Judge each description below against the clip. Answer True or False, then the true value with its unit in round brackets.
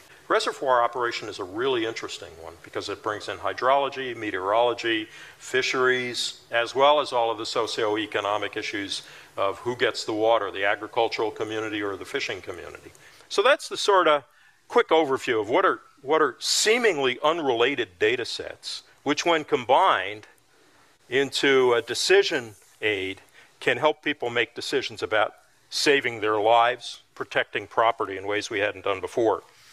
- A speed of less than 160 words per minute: True (150 wpm)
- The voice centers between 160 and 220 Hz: False (135 Hz)